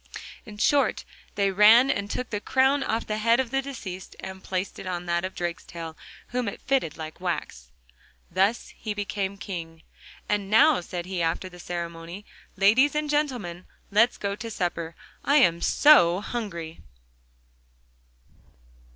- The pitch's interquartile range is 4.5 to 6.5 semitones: Yes, average, 5.2 semitones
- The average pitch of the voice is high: Yes, high, 200 Hz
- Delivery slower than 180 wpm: Yes, average, 150 wpm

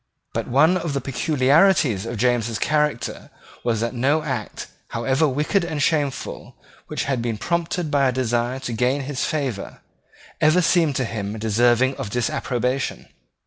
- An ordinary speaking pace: Yes, average, 150 wpm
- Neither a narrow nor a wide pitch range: Yes, average, 4.1 semitones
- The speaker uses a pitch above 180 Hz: No, low, 130 Hz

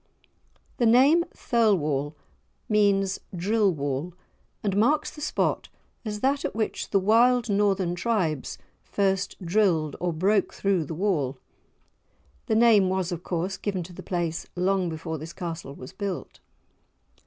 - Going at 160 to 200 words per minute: No, average, 140 wpm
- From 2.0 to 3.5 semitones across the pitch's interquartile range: No, average, 4.2 semitones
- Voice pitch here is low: No, high, 190 Hz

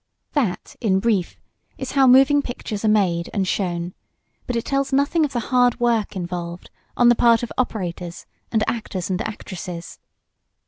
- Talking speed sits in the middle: Yes, average, 165 wpm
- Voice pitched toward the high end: Yes, high, 220 Hz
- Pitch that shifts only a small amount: No, average, 5.3 semitones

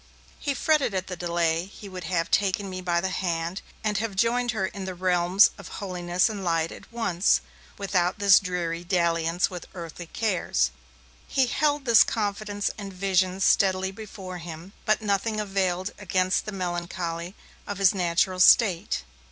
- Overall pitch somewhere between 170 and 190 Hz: Yes, medium, 185 Hz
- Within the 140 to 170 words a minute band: Yes, average, 160 wpm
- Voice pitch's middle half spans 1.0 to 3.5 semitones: Yes, narrow, 2.6 semitones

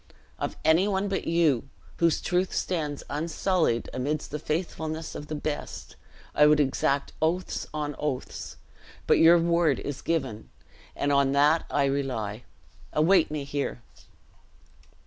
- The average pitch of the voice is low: No, medium, 150 Hz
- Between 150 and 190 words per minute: No, slow, 135 wpm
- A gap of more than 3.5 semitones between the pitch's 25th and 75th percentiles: No, average, 3.0 semitones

